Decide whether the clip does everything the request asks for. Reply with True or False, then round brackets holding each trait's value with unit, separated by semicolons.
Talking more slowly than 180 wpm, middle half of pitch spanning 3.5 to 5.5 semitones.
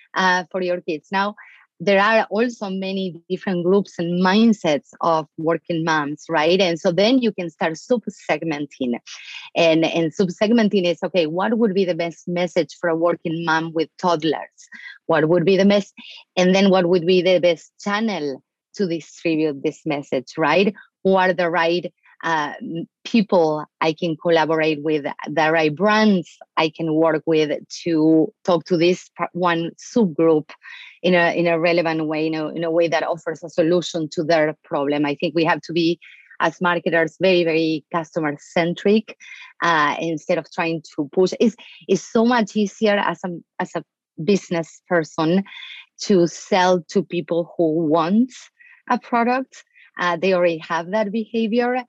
False (170 wpm; 3.1 semitones)